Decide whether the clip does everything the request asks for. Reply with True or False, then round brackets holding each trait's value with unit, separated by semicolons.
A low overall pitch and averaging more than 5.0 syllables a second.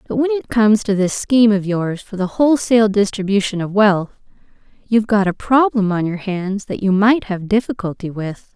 False (205 Hz; 5.4 syllables/s)